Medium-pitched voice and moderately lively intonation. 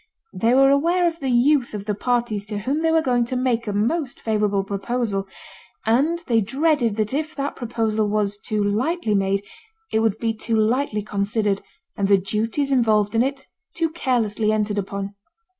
No: high, 225 Hz; average, 4.4 semitones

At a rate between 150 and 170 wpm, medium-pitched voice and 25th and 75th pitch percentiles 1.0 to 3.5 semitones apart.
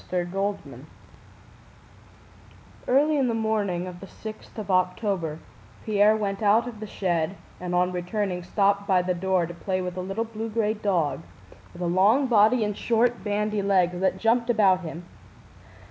No: average, 165 wpm; high, 200 Hz; average, 3.2 semitones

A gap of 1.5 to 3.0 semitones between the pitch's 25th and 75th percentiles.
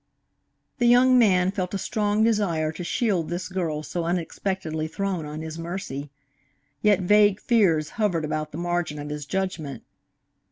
No: average, 4.5 semitones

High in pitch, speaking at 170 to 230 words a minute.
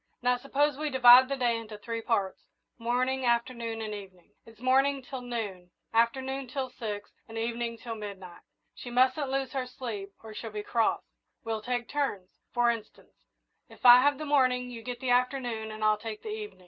Yes: high, 240 Hz; average, 185 wpm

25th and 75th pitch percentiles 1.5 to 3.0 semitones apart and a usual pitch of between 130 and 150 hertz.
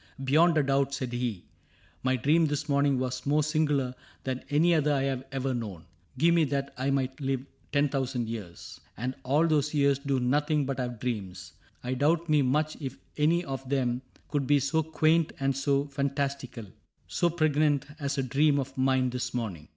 Yes: narrow, 2.5 semitones; medium, 140 Hz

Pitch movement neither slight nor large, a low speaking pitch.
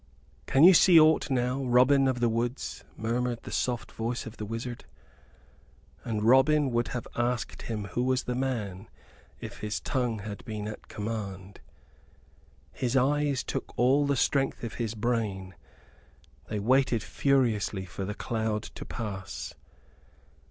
Yes: average, 3.4 semitones; low, 120 Hz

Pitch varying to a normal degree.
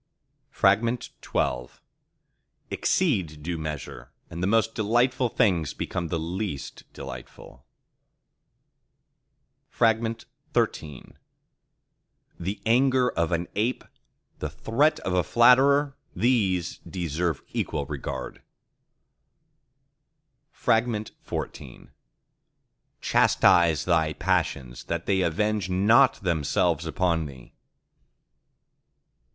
No: wide, 6.0 semitones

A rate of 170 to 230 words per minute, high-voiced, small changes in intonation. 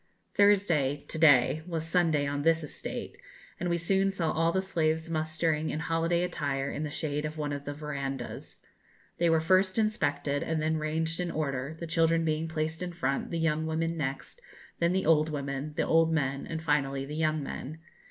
No: average, 190 wpm; medium, 160 Hz; narrow, 2.2 semitones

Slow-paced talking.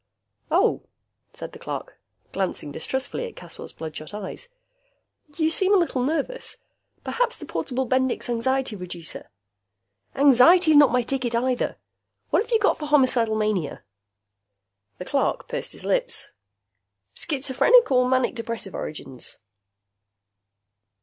Yes: slow, 125 wpm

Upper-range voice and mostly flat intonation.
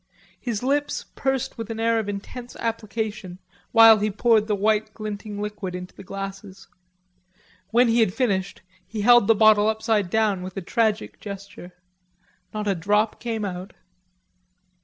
Yes: high, 215 Hz; narrow, 2.3 semitones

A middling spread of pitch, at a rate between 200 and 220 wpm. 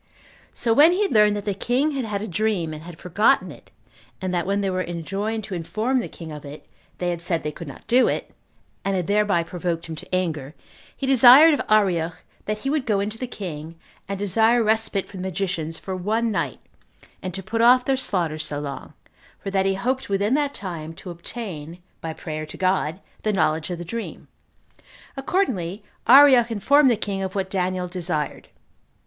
Yes: average, 4.8 semitones; fast, 205 wpm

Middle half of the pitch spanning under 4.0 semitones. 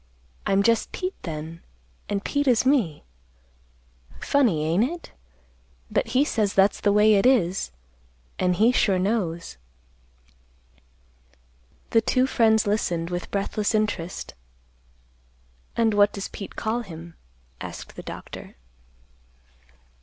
No: average, 4.3 semitones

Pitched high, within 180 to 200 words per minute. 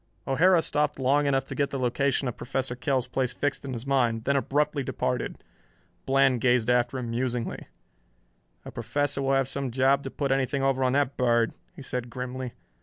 No: low, 135 Hz; average, 185 wpm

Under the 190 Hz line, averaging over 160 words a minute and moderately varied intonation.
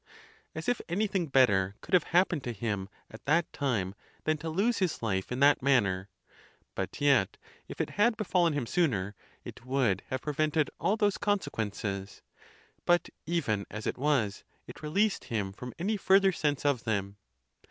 No: medium, 140 Hz; average, 170 wpm; wide, 8.5 semitones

